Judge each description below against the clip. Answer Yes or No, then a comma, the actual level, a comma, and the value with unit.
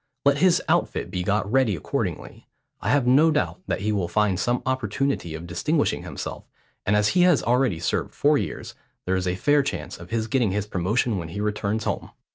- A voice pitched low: Yes, low, 105 Hz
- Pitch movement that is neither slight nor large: No, wide, 6.1 semitones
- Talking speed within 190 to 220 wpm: Yes, fast, 205 wpm